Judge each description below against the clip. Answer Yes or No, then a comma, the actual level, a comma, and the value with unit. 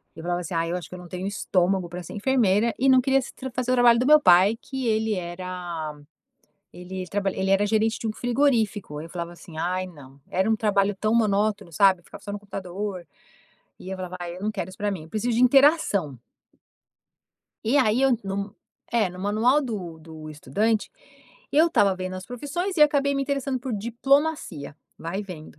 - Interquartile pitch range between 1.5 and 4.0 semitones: No, average, 5.1 semitones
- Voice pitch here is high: Yes, high, 200 Hz